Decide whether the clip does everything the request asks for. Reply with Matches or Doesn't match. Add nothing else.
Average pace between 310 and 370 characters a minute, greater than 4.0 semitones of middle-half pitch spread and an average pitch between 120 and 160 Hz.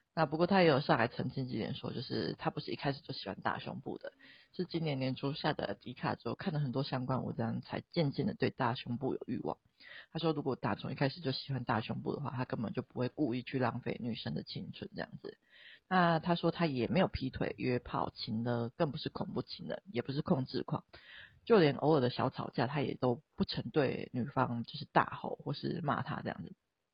Matches